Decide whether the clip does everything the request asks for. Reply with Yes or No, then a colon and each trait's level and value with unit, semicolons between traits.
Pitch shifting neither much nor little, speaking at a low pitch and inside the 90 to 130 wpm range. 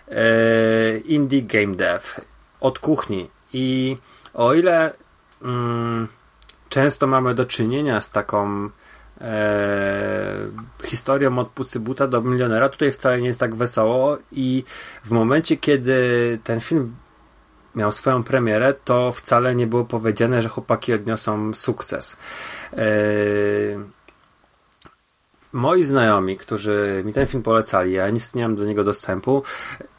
Yes: average, 3.7 semitones; low, 115 Hz; average, 120 wpm